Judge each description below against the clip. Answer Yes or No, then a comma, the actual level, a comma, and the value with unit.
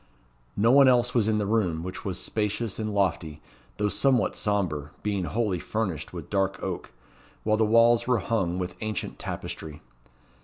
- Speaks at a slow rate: No, average, 165 wpm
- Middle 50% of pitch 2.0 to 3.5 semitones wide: No, average, 4.0 semitones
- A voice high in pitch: No, low, 105 Hz